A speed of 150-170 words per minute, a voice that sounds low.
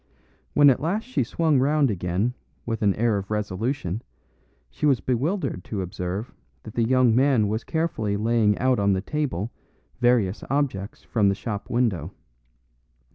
Yes: average, 155 wpm; low, 115 Hz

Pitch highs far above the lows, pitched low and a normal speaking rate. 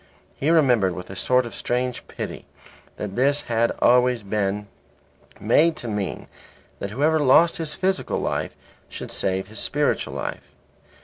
Yes: wide, 6.0 semitones; low, 125 Hz; average, 145 wpm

